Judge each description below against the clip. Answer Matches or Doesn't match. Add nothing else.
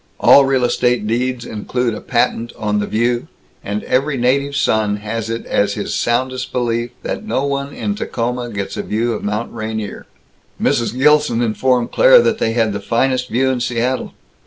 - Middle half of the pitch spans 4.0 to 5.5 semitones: Doesn't match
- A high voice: Doesn't match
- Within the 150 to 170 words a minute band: Doesn't match